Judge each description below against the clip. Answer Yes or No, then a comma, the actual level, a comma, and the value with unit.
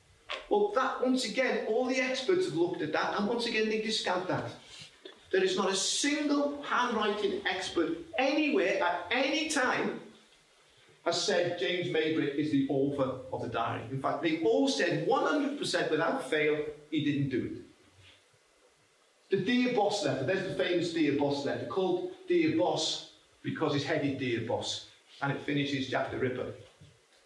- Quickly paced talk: No, average, 165 wpm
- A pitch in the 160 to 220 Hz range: Yes, high, 190 Hz